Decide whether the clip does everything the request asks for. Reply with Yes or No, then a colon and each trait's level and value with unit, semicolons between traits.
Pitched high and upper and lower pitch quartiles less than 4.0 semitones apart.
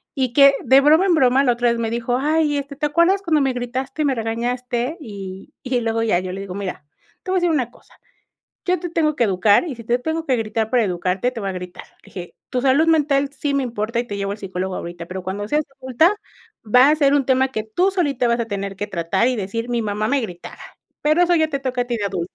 No: high, 245 Hz; wide, 5.6 semitones